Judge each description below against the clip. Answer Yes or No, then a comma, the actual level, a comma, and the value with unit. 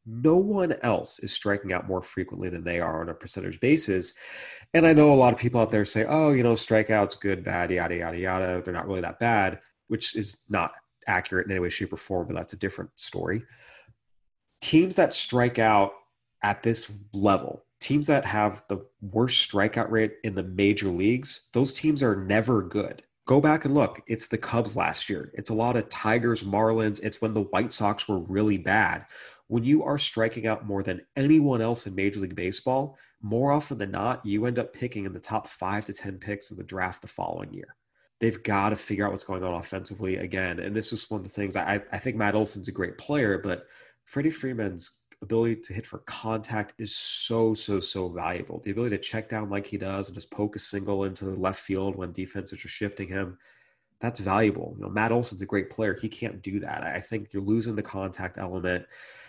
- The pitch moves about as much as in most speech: Yes, average, 3.0 semitones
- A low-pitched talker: Yes, low, 105 Hz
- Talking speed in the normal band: No, fast, 215 wpm